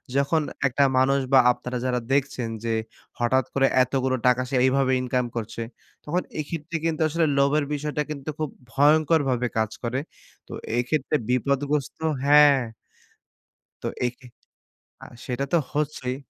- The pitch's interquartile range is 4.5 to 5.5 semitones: No, average, 2.7 semitones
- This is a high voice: No, low, 135 Hz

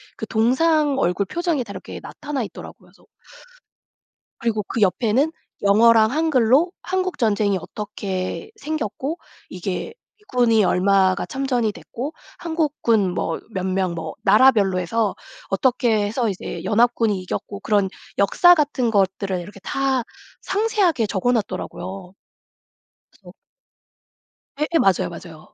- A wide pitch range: Yes, wide, 5.8 semitones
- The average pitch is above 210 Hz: Yes, high, 220 Hz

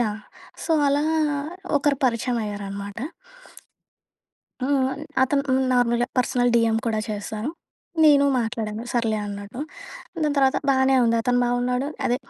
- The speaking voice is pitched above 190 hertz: Yes, high, 245 Hz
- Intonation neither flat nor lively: Yes, average, 3.3 semitones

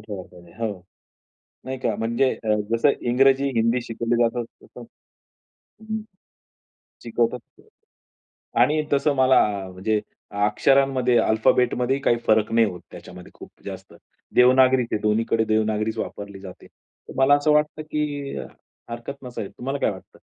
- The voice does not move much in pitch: No, average, 3.7 semitones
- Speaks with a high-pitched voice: No, low, 120 Hz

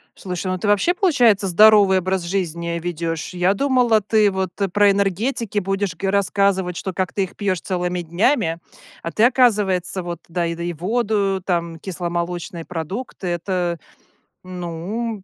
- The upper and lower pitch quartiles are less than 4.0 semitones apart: Yes, average, 3.0 semitones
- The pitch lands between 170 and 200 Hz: Yes, high, 190 Hz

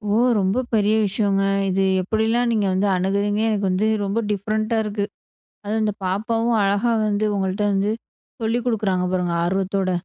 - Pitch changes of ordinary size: No, narrow, 2.1 semitones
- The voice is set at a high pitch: Yes, high, 205 Hz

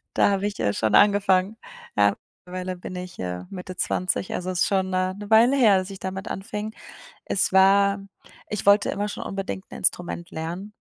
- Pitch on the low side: No, high, 190 Hz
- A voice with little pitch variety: Yes, narrow, 1.9 semitones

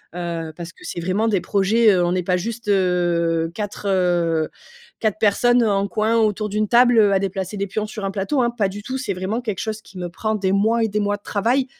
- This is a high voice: Yes, high, 200 Hz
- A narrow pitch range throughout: No, average, 3.1 semitones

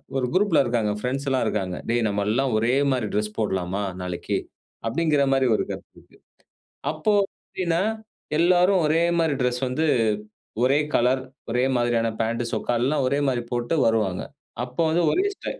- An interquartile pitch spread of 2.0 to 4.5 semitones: No, average, 5.1 semitones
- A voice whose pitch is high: No, low, 125 Hz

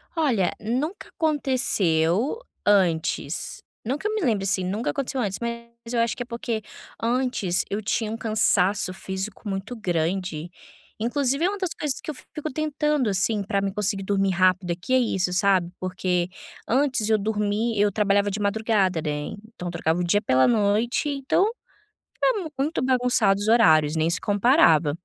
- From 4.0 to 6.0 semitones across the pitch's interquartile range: Yes, average, 5.0 semitones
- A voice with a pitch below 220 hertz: Yes, high, 210 Hz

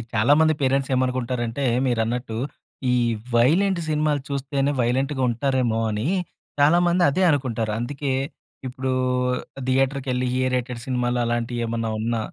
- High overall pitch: No, low, 130 Hz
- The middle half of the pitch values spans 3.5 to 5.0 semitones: No, average, 2.8 semitones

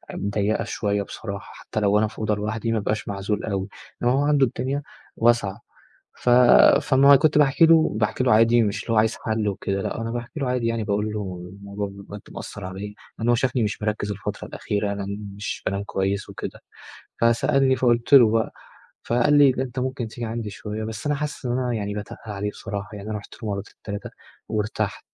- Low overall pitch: Yes, low, 110 Hz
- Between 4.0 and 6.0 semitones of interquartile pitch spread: No, average, 3.2 semitones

